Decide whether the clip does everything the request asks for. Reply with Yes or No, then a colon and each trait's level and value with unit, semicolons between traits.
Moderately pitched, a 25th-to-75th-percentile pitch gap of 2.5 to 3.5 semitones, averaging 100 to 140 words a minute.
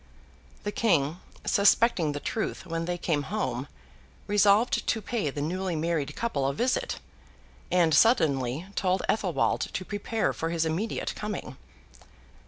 No: medium, 180 Hz; average, 5.1 semitones; slow, 135 wpm